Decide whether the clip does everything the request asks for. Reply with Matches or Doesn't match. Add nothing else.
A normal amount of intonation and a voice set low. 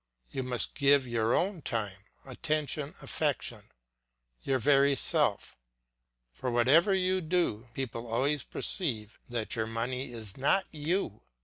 Matches